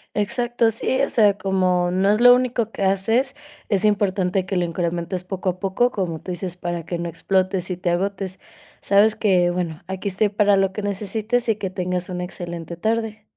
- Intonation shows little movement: No, average, 3.0 semitones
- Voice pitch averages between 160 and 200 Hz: Yes, high, 190 Hz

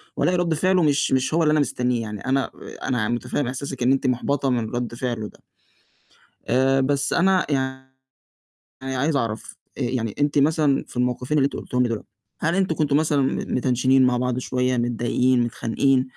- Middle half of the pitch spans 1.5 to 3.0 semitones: Yes, narrow, 2.6 semitones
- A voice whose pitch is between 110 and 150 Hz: Yes, low, 130 Hz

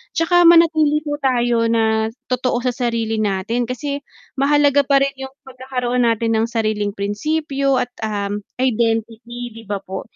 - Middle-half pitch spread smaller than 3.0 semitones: No, average, 3.7 semitones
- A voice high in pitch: Yes, high, 245 Hz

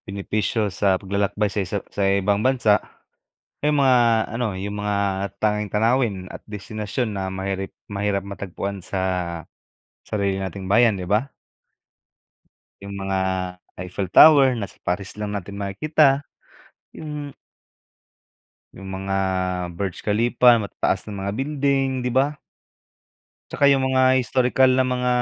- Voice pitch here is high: No, low, 105 Hz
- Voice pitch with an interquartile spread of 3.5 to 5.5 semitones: Yes, average, 4.6 semitones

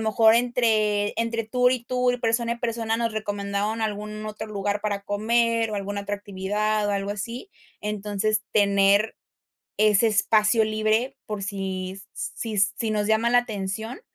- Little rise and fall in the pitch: Yes, narrow, 2.0 semitones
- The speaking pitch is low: No, high, 215 Hz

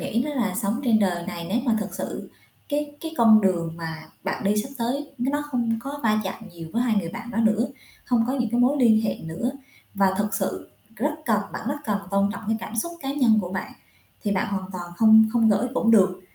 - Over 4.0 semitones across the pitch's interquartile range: No, average, 3.7 semitones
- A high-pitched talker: Yes, high, 220 Hz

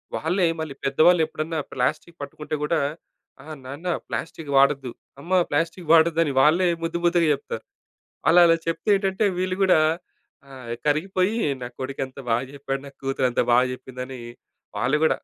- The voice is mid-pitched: Yes, medium, 155 Hz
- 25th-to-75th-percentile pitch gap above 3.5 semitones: Yes, average, 4.0 semitones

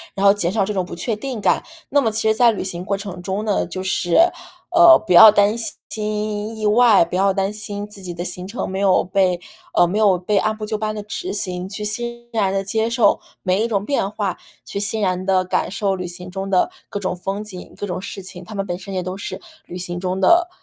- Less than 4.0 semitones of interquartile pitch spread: Yes, narrow, 2.5 semitones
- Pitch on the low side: No, high, 200 Hz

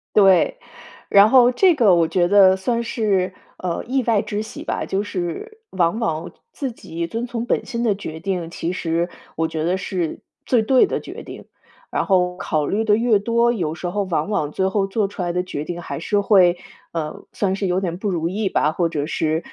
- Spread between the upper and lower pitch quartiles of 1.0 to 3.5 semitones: No, average, 4.3 semitones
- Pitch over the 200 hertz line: No, high, 190 Hz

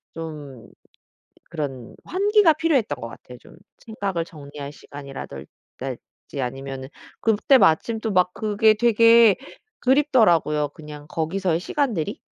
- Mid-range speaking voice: Yes, medium, 175 Hz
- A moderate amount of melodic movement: No, wide, 7.8 semitones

